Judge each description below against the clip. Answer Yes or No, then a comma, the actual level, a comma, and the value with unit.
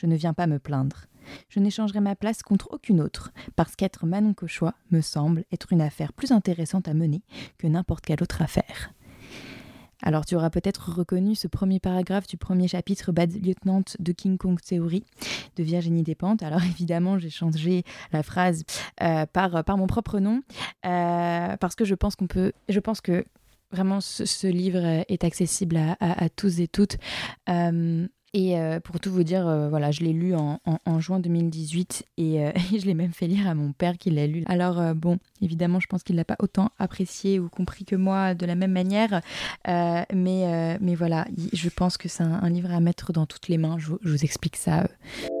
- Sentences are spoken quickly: No, average, 210 wpm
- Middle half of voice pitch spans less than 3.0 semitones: Yes, narrow, 2.4 semitones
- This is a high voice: No, medium, 175 Hz